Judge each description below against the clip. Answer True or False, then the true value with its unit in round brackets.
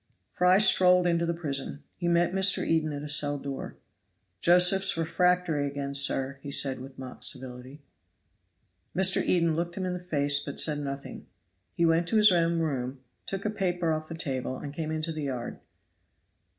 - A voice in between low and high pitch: True (160 Hz)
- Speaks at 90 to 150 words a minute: False (175 wpm)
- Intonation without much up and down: False (4.1 semitones)